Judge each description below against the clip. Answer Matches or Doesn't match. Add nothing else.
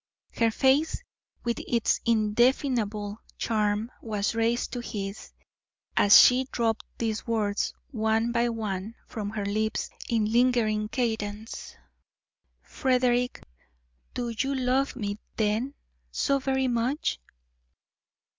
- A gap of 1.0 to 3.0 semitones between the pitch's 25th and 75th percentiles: Matches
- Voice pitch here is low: Doesn't match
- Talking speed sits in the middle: Doesn't match